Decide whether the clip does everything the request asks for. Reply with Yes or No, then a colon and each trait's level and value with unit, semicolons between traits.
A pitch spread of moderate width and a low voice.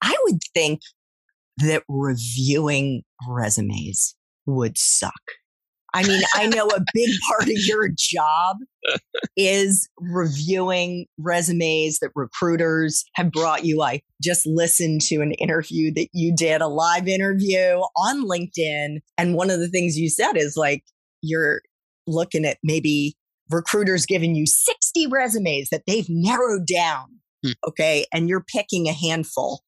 No: average, 3.5 semitones; medium, 170 Hz